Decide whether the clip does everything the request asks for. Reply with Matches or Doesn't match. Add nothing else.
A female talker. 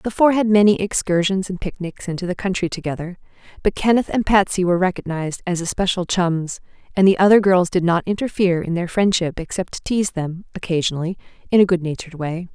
Matches